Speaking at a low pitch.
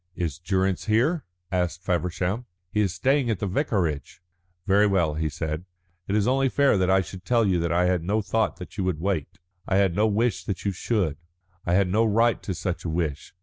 Yes: very low, 95 Hz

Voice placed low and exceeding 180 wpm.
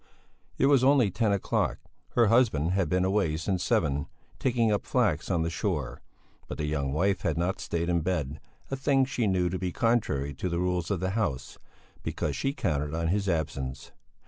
Yes: very low, 90 Hz; average, 195 wpm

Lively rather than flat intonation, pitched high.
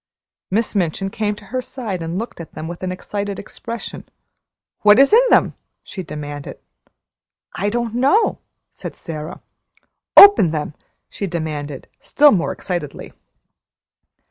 Yes: wide, 5.8 semitones; high, 195 Hz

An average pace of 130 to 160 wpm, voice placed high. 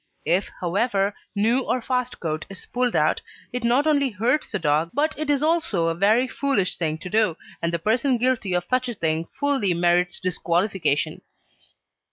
No: average, 180 wpm; high, 205 Hz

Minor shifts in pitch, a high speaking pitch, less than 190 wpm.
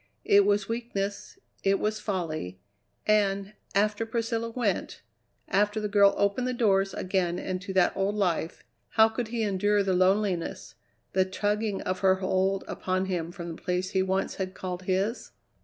Yes: narrow, 2.1 semitones; high, 195 Hz; average, 160 wpm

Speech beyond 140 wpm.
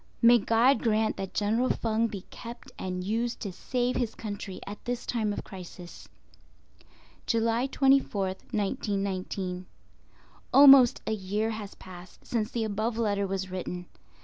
No: slow, 135 wpm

